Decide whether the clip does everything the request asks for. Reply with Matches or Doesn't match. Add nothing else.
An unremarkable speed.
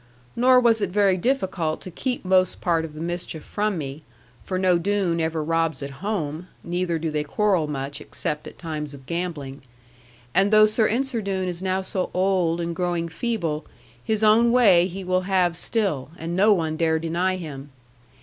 Matches